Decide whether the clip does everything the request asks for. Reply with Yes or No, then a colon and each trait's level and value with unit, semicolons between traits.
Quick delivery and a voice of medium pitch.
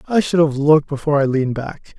Yes: fast, 240 wpm; medium, 150 Hz